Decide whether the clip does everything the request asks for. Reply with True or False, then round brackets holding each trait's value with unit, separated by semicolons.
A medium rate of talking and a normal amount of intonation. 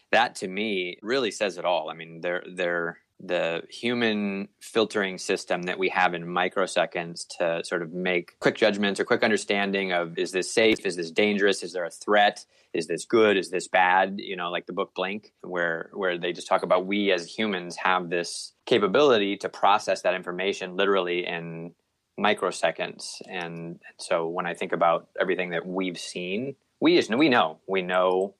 False (185 wpm; 2.3 semitones)